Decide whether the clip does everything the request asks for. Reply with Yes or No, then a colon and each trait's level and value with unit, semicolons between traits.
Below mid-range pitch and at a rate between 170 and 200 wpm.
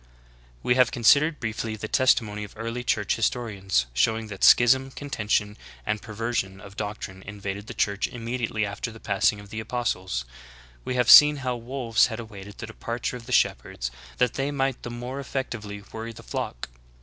Yes: low, 115 Hz; average, 185 wpm